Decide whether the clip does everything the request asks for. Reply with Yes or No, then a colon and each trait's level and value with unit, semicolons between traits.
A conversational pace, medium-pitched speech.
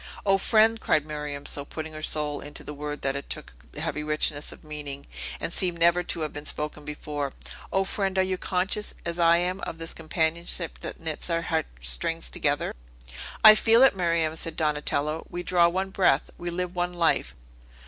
Yes: average, 195 wpm; medium, 165 Hz